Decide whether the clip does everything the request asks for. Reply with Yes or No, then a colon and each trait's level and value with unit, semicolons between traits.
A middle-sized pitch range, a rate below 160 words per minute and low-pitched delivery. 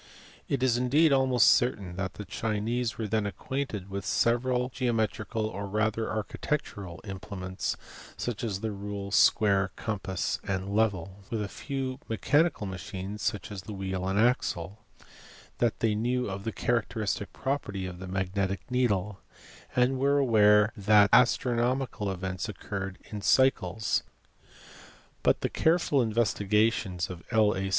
Yes: average, 3.9 semitones; slow, 135 wpm; low, 105 Hz